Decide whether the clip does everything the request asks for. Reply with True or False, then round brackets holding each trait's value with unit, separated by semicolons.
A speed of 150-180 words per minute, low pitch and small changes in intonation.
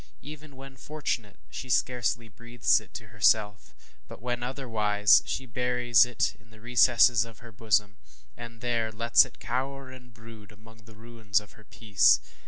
True (165 wpm; 115 Hz; 2.3 semitones)